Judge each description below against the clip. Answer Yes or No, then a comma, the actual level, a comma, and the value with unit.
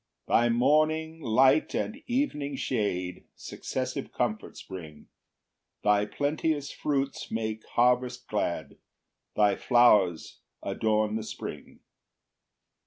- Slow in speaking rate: Yes, slow, 100 wpm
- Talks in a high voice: No, low, 120 Hz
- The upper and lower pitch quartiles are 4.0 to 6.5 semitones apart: Yes, wide, 5.4 semitones